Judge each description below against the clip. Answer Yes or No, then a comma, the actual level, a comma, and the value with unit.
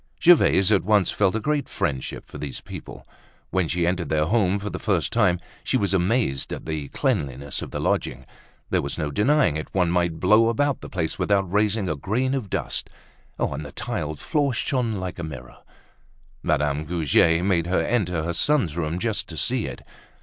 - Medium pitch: No, very low, 90 Hz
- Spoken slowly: No, average, 195 wpm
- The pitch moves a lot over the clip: Yes, wide, 5.8 semitones